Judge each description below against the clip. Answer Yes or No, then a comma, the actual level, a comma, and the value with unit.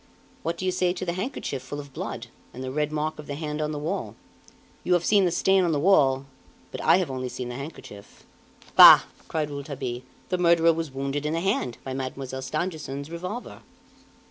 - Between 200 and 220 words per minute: Yes, fast, 205 wpm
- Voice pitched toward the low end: No, medium, 150 Hz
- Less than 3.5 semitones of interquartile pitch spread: No, average, 4.4 semitones